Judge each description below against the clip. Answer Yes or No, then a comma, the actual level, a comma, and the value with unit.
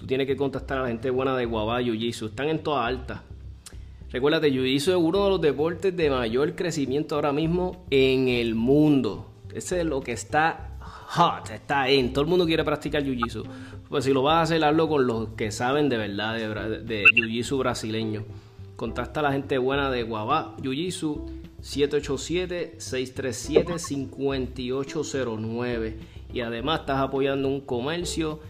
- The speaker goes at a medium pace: Yes, average, 170 wpm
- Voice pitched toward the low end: Yes, low, 130 Hz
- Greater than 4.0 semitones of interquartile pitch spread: Yes, average, 4.7 semitones